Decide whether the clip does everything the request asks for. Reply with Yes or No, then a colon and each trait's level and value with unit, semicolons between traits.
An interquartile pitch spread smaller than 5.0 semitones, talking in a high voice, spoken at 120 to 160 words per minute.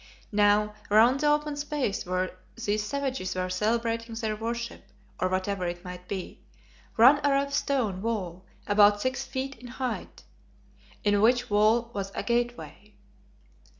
Yes: average, 3.9 semitones; high, 225 Hz; average, 145 wpm